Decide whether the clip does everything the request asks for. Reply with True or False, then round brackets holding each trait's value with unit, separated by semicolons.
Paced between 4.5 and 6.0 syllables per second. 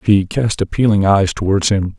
True (4.9 syllables/s)